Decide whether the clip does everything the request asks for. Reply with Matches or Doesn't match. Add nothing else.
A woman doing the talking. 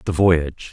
Doesn't match